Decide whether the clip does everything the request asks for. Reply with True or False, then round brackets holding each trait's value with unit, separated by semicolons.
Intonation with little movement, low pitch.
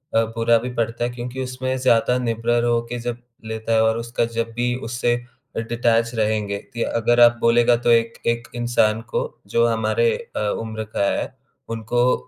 True (1.1 semitones; 115 Hz)